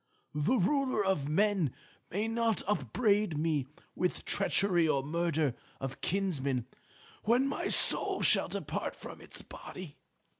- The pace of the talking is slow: Yes, slow, 125 wpm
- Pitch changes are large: Yes, wide, 5.9 semitones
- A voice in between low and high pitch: Yes, medium, 180 Hz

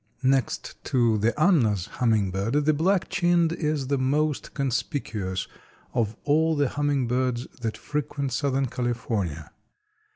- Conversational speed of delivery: No, slow, 120 wpm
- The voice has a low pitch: Yes, low, 130 Hz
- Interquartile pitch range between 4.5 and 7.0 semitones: Yes, average, 4.8 semitones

